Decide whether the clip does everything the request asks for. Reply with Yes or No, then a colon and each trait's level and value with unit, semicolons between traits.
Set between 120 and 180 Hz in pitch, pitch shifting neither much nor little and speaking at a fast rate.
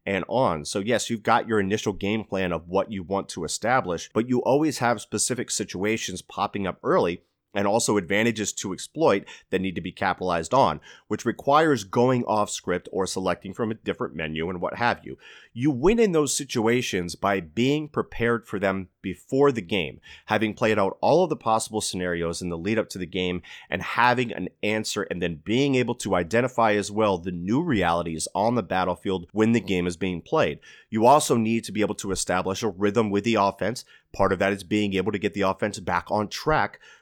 No: low, 105 Hz; average, 3.6 semitones; fast, 210 wpm